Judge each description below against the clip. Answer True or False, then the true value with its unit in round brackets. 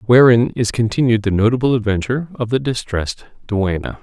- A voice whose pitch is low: True (115 Hz)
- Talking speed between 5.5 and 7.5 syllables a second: True (5.6 syllables/s)